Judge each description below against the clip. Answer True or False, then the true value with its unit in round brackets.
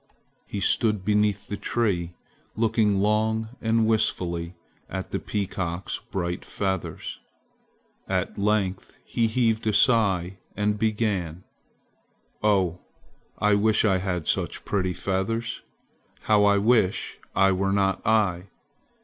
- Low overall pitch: True (100 Hz)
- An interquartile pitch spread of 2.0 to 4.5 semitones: True (2.7 semitones)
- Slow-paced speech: True (115 wpm)